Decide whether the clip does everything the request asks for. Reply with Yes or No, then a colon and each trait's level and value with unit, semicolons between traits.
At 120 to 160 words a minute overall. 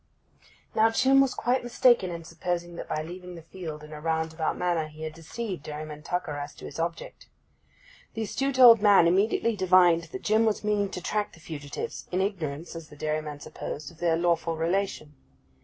No: average, 190 wpm